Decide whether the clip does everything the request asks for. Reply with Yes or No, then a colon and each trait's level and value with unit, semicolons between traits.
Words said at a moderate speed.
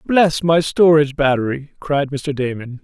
Yes: average, 150 wpm